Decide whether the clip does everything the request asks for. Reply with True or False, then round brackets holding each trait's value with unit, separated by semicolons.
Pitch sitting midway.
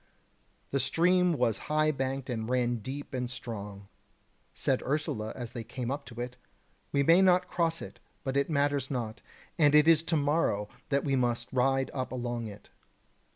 False (130 Hz)